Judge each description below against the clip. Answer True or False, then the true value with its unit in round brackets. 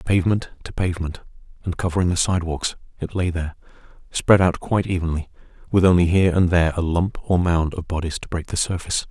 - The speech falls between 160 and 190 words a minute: False (200 wpm)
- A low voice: True (90 Hz)